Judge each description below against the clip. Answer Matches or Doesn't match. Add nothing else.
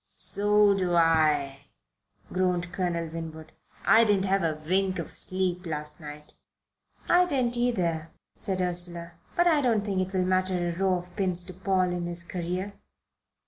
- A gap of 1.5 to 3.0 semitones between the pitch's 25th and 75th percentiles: Matches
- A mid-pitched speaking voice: Matches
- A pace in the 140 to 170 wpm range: Matches